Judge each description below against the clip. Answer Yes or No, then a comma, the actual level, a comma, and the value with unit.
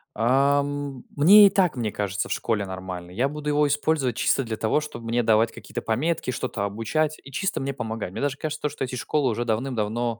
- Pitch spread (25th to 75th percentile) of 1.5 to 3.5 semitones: No, average, 4.7 semitones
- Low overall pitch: Yes, low, 125 Hz